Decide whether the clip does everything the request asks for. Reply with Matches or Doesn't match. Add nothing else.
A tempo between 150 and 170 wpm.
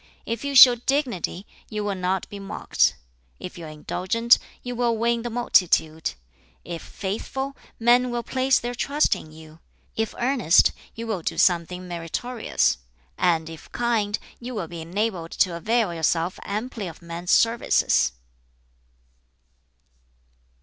Doesn't match